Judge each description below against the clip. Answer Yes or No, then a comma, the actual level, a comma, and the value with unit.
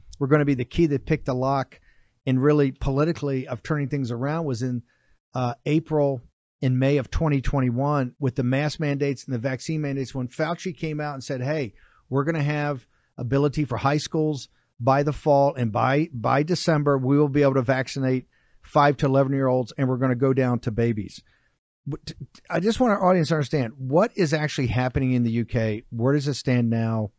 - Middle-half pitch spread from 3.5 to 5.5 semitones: No, average, 2.7 semitones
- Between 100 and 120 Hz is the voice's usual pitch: No, medium, 140 Hz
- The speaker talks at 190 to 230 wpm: Yes, fast, 205 wpm